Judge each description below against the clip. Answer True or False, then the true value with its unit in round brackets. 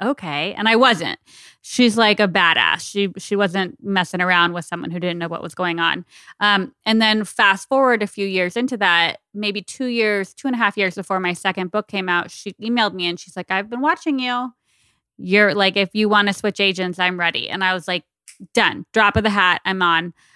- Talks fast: True (225 wpm)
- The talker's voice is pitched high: True (195 Hz)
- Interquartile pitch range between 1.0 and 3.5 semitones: True (3.0 semitones)